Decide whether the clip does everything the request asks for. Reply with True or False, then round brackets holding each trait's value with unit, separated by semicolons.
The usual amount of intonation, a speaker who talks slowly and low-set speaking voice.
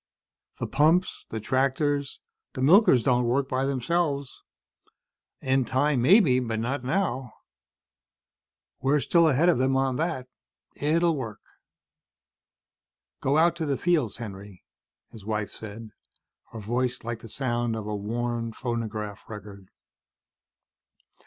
True (4.2 semitones; 120 wpm; 130 Hz)